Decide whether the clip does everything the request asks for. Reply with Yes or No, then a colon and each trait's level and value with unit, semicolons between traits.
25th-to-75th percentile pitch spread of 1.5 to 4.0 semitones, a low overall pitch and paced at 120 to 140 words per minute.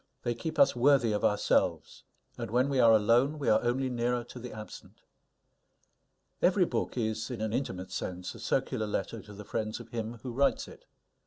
No: narrow, 2.6 semitones; low, 115 Hz; average, 190 wpm